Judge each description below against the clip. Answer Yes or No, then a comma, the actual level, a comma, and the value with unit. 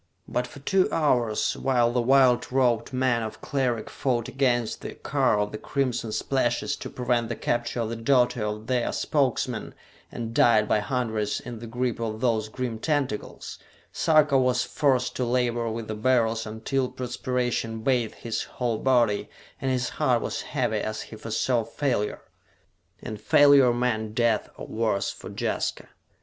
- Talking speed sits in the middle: Yes, average, 160 wpm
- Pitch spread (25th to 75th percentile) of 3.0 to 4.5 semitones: No, narrow, 2.4 semitones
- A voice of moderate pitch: No, low, 120 Hz